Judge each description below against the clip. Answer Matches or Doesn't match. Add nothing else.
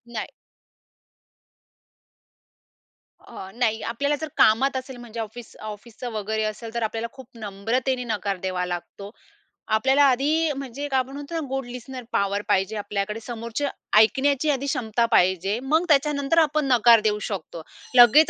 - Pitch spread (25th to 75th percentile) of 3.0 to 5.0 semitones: Matches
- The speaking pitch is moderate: Doesn't match